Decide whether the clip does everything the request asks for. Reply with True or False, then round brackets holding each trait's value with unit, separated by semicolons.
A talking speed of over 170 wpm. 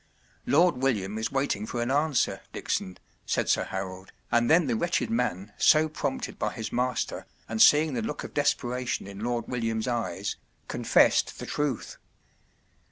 False (165 wpm)